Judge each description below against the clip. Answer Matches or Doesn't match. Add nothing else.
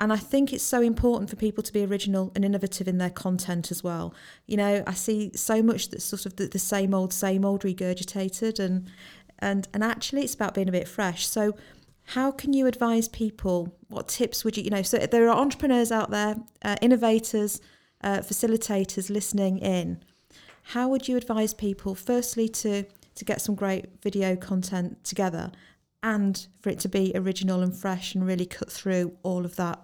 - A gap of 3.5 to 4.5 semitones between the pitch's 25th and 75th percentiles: Doesn't match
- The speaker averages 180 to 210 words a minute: Matches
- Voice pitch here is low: Doesn't match